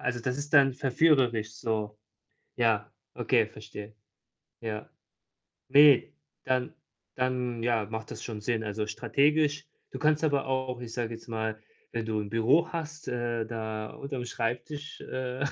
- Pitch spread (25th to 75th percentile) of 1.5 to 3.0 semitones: No, average, 3.5 semitones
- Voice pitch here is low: Yes, low, 120 Hz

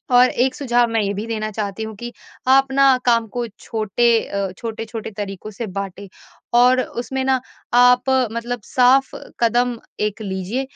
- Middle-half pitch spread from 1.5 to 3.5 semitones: Yes, average, 2.8 semitones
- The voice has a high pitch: Yes, high, 235 Hz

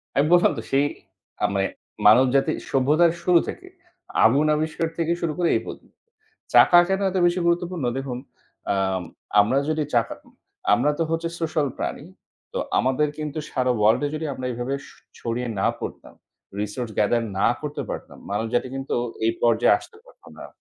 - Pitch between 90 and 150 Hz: Yes, medium, 140 Hz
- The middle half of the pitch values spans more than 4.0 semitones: Yes, wide, 5.6 semitones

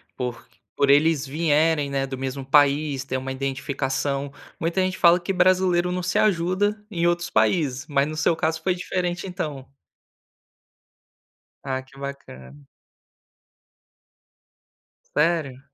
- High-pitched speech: No, medium, 150 Hz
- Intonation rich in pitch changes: No, average, 4.2 semitones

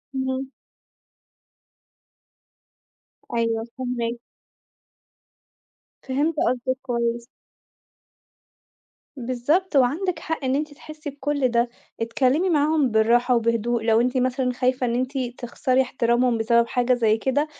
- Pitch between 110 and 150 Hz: No, very high, 255 Hz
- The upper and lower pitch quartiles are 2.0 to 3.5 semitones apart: Yes, narrow, 2.6 semitones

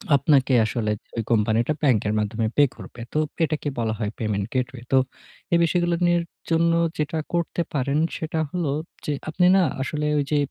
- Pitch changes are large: Yes, wide, 5.7 semitones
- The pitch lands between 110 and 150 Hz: Yes, medium, 140 Hz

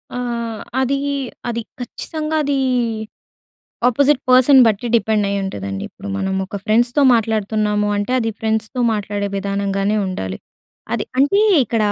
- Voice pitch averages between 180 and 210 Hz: No, high, 220 Hz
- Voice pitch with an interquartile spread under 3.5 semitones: No, average, 3.8 semitones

